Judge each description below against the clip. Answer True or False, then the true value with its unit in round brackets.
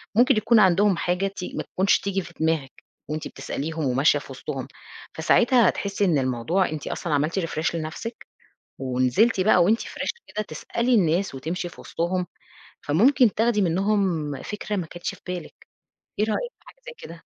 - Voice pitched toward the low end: False (185 Hz)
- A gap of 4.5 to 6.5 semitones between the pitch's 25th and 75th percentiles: True (4.9 semitones)